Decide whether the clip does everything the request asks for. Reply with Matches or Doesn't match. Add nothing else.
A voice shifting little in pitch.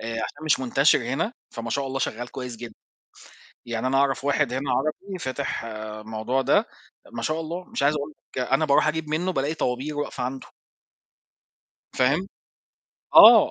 Doesn't match